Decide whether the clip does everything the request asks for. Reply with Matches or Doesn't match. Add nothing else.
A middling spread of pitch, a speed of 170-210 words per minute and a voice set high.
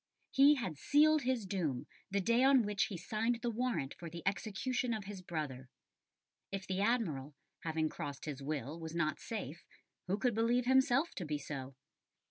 Doesn't match